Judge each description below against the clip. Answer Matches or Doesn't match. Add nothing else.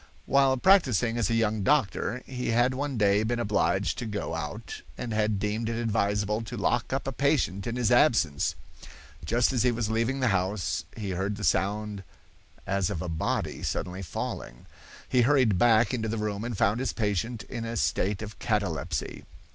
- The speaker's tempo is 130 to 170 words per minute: Doesn't match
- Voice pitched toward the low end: Matches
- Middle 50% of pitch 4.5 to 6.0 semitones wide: Doesn't match